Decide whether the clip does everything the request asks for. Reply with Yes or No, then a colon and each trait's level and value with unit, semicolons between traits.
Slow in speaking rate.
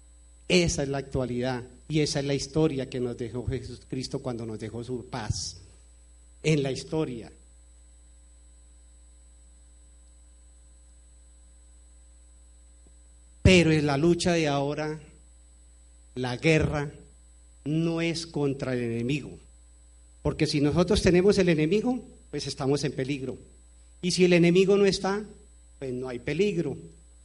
Yes: slow, 120 wpm